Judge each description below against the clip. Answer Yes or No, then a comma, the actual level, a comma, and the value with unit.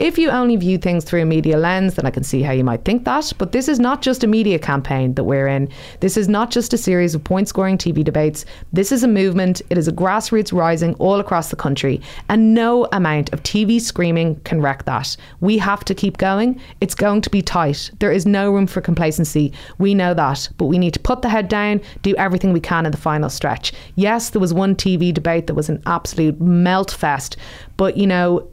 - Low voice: No, medium, 185 Hz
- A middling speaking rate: No, fast, 235 wpm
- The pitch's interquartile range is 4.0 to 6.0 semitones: Yes, average, 4.3 semitones